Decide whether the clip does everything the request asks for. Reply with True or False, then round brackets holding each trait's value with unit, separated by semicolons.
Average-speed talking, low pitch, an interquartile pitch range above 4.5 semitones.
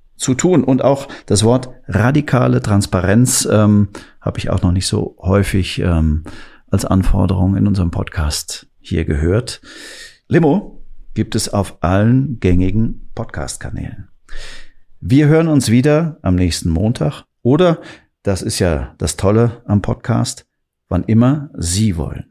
True (135 wpm; 105 Hz; 5.3 semitones)